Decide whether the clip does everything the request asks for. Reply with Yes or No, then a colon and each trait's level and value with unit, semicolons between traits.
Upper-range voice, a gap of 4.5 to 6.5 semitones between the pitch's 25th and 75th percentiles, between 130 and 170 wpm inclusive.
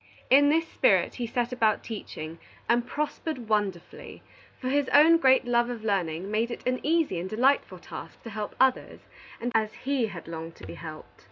No: high, 235 Hz; average, 5.0 semitones; average, 180 wpm